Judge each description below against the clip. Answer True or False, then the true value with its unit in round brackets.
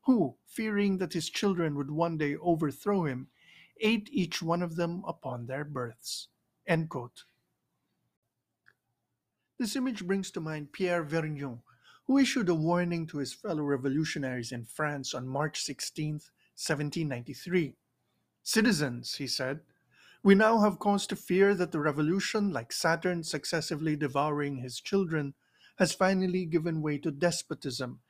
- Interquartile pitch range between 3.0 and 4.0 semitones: False (4.5 semitones)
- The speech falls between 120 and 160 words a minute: True (140 wpm)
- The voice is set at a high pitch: False (165 Hz)